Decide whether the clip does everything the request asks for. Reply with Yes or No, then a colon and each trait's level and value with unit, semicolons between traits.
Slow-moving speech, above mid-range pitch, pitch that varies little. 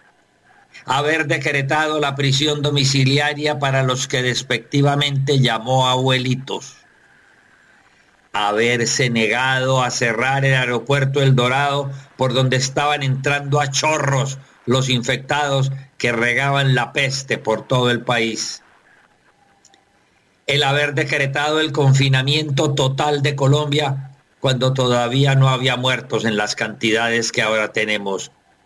No: slow, 115 wpm; low, 135 Hz; narrow, 2.2 semitones